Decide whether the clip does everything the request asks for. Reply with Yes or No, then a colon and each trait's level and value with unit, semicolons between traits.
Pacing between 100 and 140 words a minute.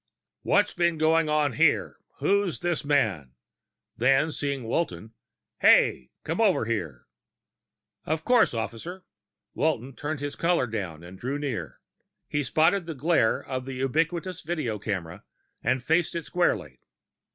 Yes: slow, 135 wpm